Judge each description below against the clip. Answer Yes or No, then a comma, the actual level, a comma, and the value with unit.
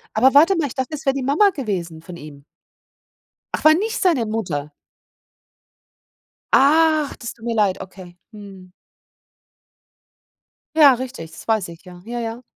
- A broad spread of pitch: Yes, wide, 7.6 semitones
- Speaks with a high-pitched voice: Yes, high, 230 Hz